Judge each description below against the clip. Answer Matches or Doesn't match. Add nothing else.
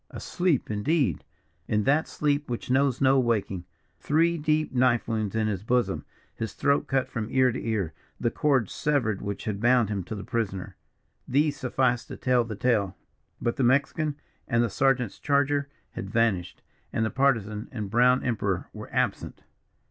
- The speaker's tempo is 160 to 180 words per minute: Matches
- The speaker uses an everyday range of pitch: Matches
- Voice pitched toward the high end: Doesn't match